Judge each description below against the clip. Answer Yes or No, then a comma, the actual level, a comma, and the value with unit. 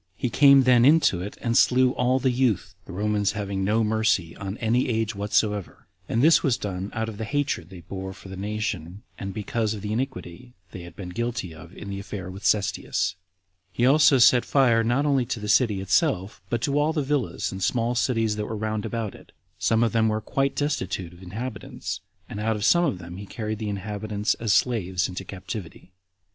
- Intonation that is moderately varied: Yes, average, 4.1 semitones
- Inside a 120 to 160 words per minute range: No, fast, 205 wpm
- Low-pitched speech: Yes, low, 110 Hz